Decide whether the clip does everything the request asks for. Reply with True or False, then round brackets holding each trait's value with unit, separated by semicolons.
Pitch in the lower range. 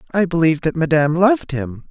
False (165 Hz)